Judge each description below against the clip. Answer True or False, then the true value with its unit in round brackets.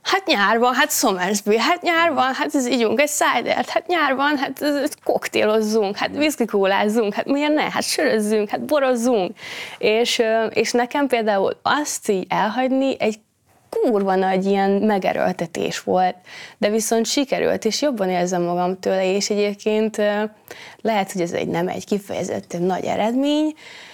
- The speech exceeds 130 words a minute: True (150 wpm)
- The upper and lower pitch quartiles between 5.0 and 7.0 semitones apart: True (5.6 semitones)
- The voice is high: True (225 Hz)